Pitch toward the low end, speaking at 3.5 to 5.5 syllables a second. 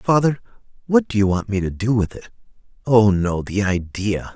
Yes: low, 105 Hz; 4.8 syllables/s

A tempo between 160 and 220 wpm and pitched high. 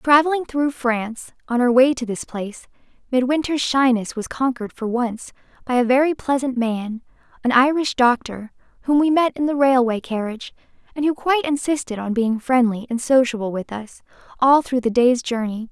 Yes: average, 170 wpm; very high, 250 Hz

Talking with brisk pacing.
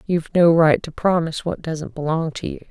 Yes: fast, 220 wpm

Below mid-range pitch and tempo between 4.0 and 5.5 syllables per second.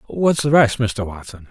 Yes: low, 120 Hz; 4.5 syllables/s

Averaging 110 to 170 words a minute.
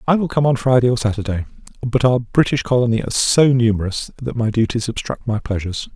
No: average, 200 wpm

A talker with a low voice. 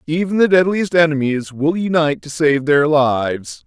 No: medium, 150 Hz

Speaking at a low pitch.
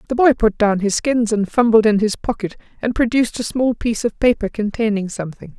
No: high, 220 Hz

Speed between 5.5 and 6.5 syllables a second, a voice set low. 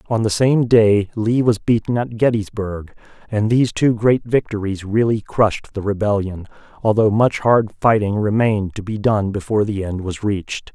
No: 4.9 syllables/s; low, 110 Hz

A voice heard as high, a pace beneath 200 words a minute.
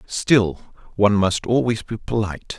No: low, 105 Hz; average, 140 wpm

